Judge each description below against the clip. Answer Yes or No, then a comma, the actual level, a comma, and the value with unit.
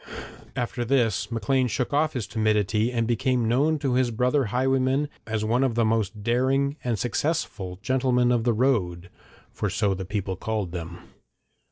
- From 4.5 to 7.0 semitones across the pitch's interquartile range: No, average, 3.5 semitones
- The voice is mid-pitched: No, low, 120 Hz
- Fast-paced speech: No, average, 165 wpm